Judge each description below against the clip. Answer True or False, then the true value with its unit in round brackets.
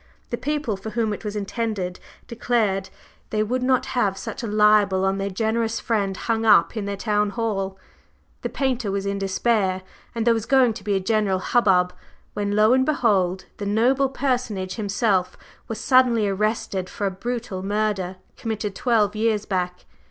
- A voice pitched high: True (210 Hz)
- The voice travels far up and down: False (2.9 semitones)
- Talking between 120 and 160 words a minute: False (175 wpm)